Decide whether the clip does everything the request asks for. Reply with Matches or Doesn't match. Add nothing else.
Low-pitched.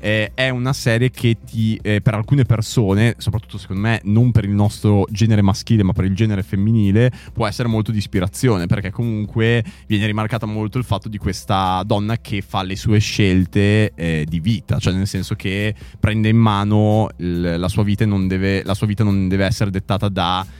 Matches